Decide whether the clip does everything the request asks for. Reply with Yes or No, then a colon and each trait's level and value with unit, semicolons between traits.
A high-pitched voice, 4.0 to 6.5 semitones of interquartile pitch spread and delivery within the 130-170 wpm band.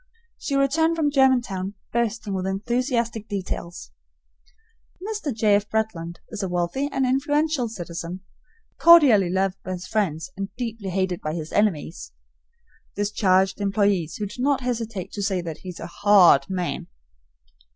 Yes: high, 205 Hz; average, 5.1 semitones; average, 150 wpm